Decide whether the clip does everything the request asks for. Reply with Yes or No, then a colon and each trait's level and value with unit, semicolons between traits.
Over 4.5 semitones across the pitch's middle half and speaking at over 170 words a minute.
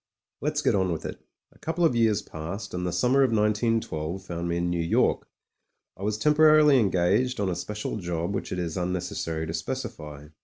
Yes: average, 5.3 semitones; average, 200 wpm